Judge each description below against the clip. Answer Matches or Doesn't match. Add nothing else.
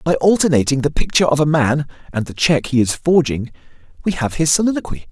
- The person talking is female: Doesn't match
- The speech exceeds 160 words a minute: Matches